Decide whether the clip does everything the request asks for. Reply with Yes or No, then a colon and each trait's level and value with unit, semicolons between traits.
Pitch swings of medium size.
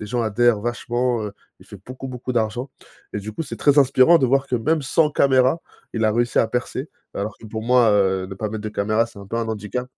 Yes: average, 3.1 semitones